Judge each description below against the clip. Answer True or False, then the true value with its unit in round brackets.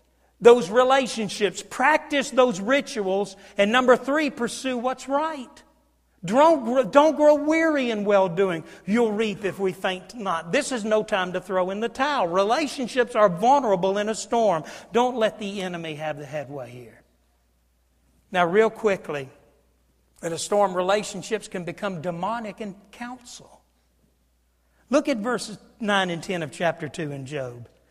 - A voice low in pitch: False (205 Hz)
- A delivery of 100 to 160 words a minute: True (150 wpm)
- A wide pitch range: True (6.6 semitones)